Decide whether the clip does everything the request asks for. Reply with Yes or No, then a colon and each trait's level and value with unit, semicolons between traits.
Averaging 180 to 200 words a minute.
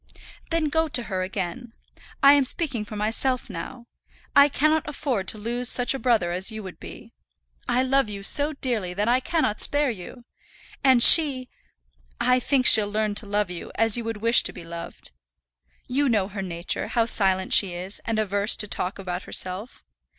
Yes: average, 185 wpm